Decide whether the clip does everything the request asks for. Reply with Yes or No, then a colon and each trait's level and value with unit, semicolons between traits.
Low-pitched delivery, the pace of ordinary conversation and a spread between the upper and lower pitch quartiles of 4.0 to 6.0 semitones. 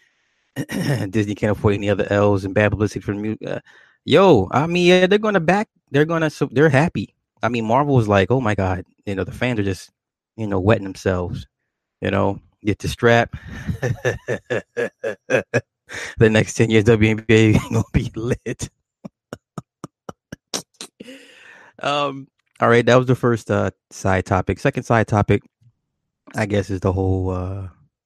Yes: low, 110 Hz; average, 160 wpm; average, 4.7 semitones